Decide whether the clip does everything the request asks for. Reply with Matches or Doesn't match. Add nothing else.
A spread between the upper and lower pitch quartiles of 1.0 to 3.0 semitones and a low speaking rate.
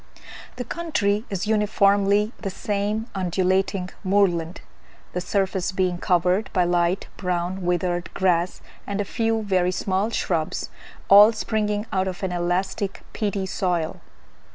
Matches